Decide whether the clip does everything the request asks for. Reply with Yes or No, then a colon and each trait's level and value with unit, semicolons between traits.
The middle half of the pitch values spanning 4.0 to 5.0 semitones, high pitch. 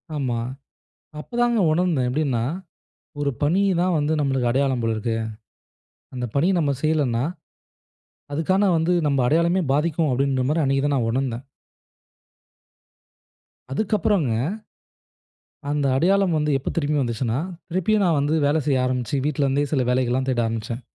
No: average, 4.3 semitones; medium, 140 Hz